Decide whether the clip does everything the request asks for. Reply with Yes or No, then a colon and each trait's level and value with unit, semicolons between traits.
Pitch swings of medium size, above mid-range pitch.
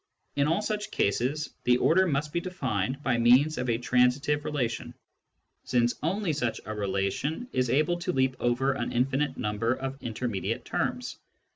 No: average, 4.1 semitones; low, 130 Hz